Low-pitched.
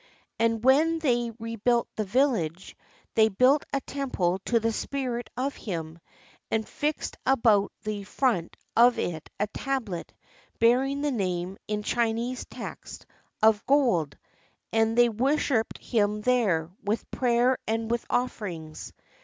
No: high, 230 Hz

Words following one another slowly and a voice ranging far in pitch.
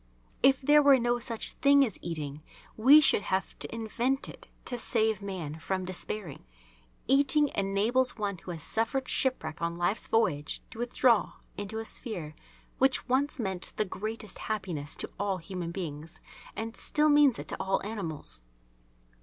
No: average, 160 wpm; wide, 5.9 semitones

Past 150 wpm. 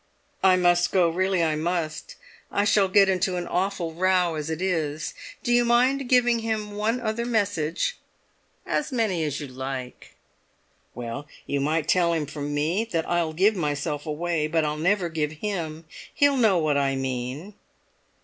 Yes: average, 165 wpm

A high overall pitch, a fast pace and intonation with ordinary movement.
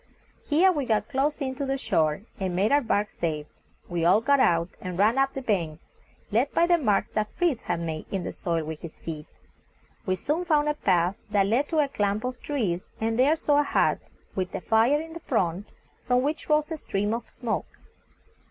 No: high, 225 Hz; fast, 210 wpm; wide, 7.8 semitones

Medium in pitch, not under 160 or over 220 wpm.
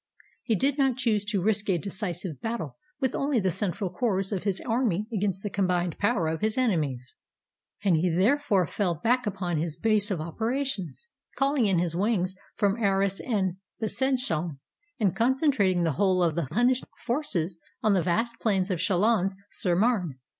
No: high, 200 Hz; average, 170 wpm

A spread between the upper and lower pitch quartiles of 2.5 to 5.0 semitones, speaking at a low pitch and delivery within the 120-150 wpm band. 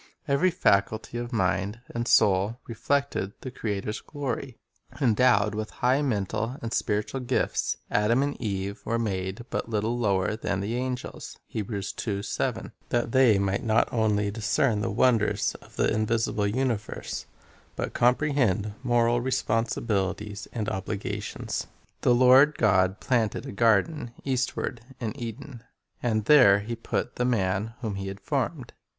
Yes: average, 3.3 semitones; low, 115 Hz; slow, 135 wpm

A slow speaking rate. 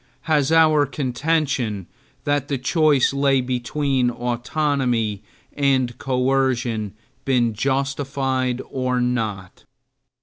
Yes: slow, 90 wpm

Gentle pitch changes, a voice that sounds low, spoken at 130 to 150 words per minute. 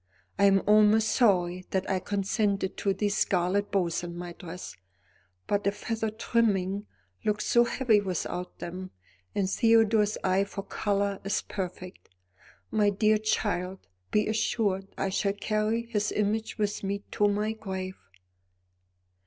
No: narrow, 2.1 semitones; high, 200 Hz; average, 140 wpm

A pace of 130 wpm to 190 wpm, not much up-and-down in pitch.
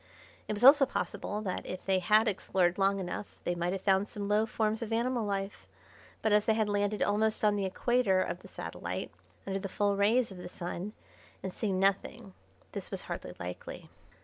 No: average, 200 wpm; narrow, 2.2 semitones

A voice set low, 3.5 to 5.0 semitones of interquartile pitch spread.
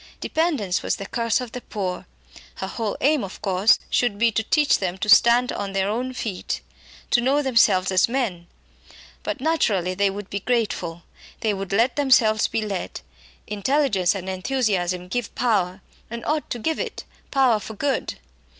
No: high, 215 Hz; average, 4.7 semitones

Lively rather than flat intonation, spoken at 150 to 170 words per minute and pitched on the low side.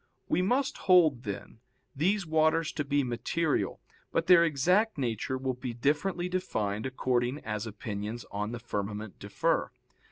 No: wide, 6.9 semitones; average, 140 wpm; low, 130 Hz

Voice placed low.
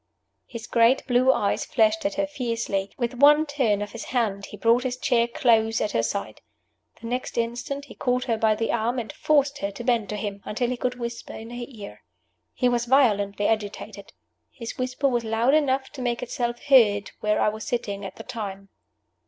No: high, 235 Hz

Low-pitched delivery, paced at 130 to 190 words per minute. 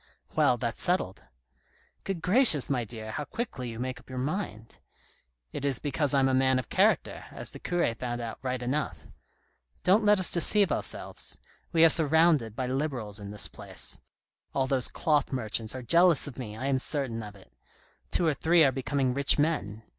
No: low, 130 Hz; average, 200 wpm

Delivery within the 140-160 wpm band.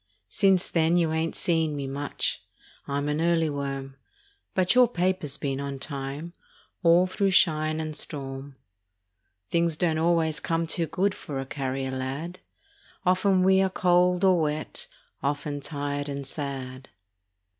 Yes: average, 145 wpm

